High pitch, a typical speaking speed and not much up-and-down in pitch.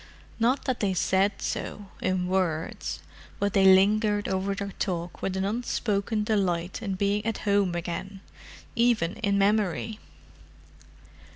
No: high, 200 Hz; slow, 125 wpm; narrow, 2.0 semitones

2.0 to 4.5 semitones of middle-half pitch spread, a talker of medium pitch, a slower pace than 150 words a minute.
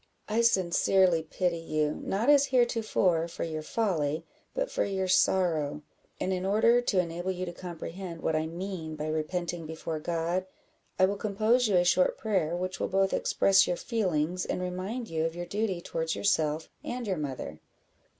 No: average, 3.3 semitones; medium, 180 Hz; average, 175 wpm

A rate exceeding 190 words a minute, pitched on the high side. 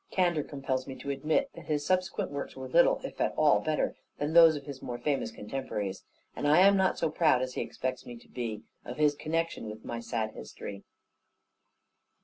No: average, 200 wpm; medium, 140 Hz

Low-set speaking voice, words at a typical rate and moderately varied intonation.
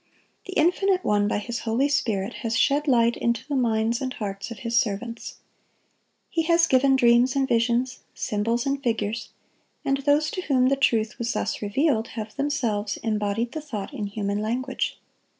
No: high, 235 Hz; average, 170 wpm; average, 4.0 semitones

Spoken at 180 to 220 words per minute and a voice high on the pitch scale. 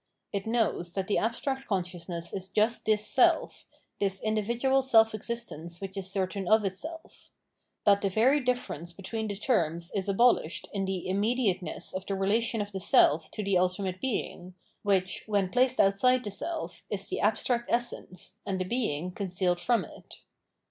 No: average, 165 wpm; high, 200 Hz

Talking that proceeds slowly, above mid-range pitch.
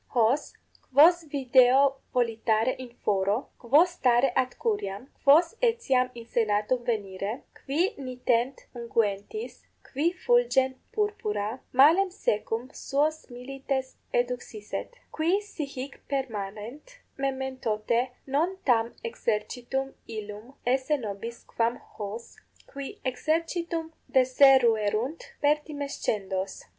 Yes: slow, 95 wpm; very high, 255 Hz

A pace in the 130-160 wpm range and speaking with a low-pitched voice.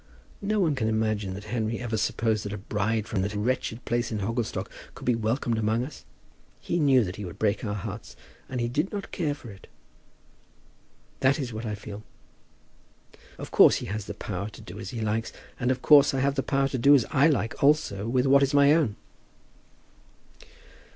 No: fast, 205 wpm; low, 115 Hz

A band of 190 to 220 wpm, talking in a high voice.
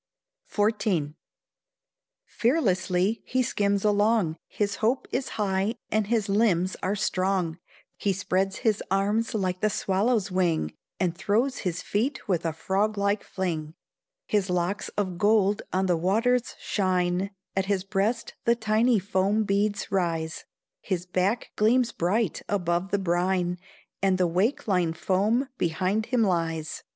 No: average, 140 wpm; high, 195 Hz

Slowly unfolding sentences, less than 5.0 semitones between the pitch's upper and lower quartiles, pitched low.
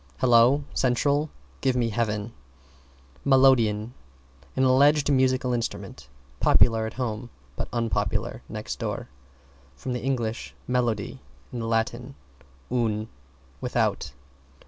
Yes: slow, 100 wpm; narrow, 2.6 semitones; low, 120 Hz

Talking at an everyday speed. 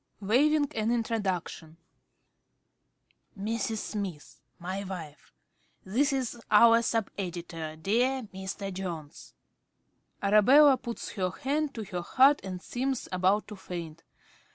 No: slow, 115 wpm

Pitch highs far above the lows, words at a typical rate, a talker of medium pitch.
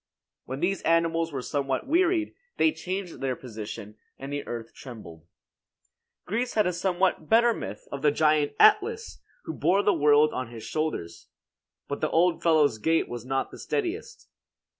Yes: wide, 6.8 semitones; average, 165 wpm; medium, 155 Hz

